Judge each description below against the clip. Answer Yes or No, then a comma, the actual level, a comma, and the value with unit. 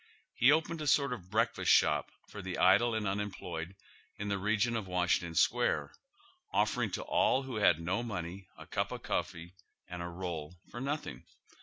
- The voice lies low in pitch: Yes, very low, 95 Hz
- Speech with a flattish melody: No, average, 5.3 semitones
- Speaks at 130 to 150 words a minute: No, average, 175 wpm